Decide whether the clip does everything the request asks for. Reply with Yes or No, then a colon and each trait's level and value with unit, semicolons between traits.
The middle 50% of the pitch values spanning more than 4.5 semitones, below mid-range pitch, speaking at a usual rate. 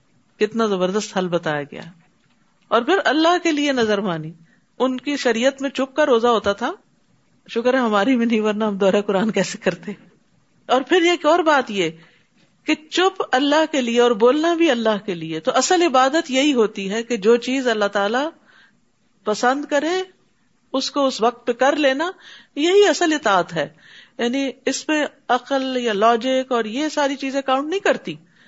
No: average, 5.2 semitones; very high, 250 Hz; average, 180 wpm